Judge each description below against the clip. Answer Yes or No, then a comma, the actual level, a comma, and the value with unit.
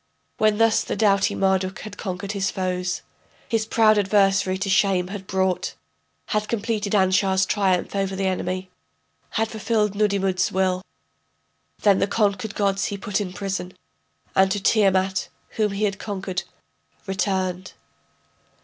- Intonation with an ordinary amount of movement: No, narrow, 1.7 semitones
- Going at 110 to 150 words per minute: Yes, average, 140 wpm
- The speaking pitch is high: Yes, high, 195 Hz